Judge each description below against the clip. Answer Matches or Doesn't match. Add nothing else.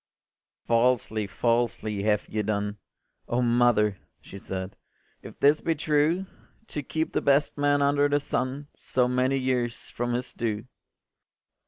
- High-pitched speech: Doesn't match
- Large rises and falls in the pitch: Doesn't match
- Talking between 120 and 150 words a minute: Matches